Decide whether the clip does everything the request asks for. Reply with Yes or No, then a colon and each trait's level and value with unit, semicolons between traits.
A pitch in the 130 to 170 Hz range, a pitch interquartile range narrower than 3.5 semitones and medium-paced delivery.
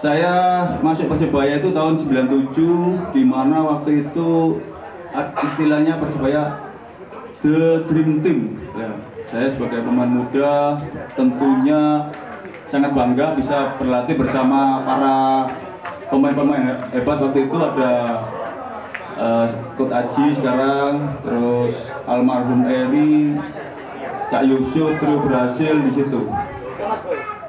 Yes: medium, 140 Hz; average, 2.8 semitones; average, 100 wpm